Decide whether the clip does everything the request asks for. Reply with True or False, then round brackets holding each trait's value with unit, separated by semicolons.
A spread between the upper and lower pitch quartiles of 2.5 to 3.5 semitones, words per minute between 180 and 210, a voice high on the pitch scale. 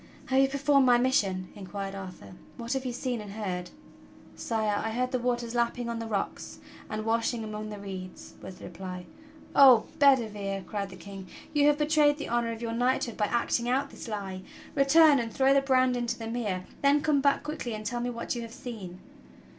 False (4.2 semitones; 205 wpm; 235 Hz)